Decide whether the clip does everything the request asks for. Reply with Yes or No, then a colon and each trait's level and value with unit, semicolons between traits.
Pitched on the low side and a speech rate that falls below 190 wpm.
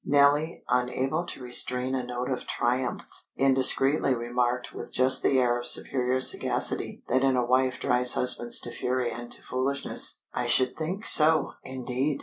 Yes: low, 130 Hz; average, 160 wpm